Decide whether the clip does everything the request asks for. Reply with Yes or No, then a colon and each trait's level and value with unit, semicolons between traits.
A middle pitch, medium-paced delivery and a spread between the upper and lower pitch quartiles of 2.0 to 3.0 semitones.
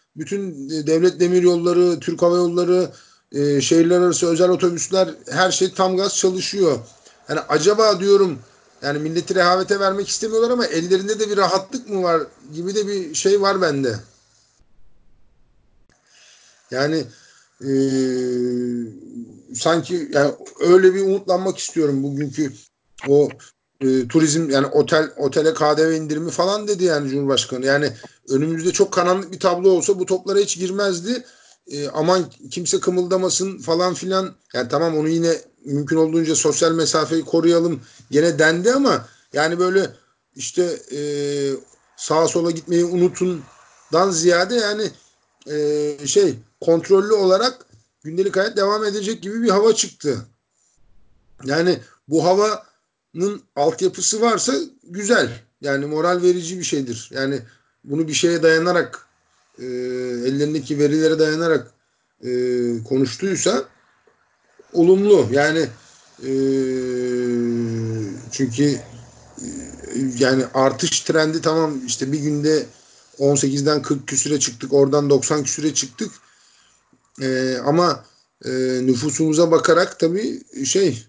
No: medium, 160 Hz; average, 115 wpm; average, 5.1 semitones